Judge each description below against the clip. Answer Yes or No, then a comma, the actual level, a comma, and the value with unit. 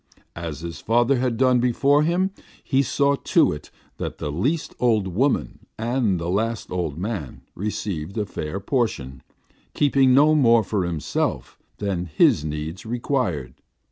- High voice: No, low, 110 Hz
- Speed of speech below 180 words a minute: Yes, average, 145 wpm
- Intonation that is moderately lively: No, wide, 7.2 semitones